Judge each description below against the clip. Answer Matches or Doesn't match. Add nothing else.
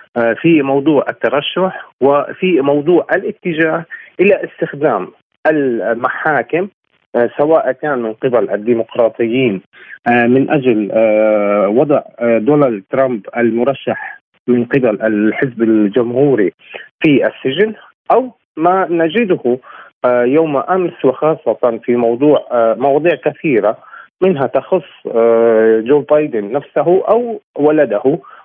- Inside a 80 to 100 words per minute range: Matches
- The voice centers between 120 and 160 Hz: Matches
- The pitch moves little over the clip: Doesn't match